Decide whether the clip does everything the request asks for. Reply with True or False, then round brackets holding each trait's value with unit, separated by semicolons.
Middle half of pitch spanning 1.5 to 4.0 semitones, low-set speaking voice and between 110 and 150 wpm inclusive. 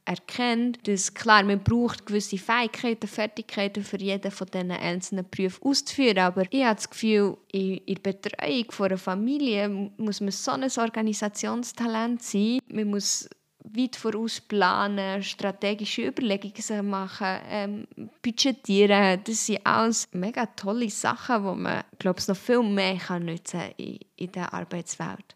False (2.9 semitones; 205 Hz; 145 wpm)